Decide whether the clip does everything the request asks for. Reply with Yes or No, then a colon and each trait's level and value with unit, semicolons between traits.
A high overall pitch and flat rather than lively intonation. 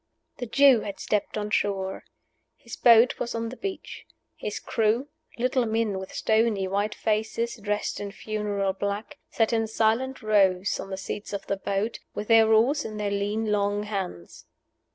Yes: high, 215 Hz; narrow, 2.2 semitones